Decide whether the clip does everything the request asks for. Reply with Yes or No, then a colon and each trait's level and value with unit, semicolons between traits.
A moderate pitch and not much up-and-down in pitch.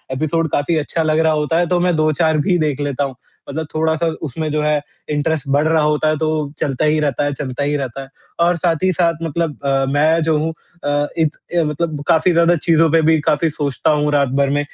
Yes: medium, 155 Hz; narrow, 1.9 semitones